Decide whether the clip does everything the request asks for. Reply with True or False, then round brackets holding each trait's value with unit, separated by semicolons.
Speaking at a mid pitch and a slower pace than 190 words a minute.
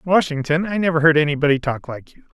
False (155 Hz; 200 wpm)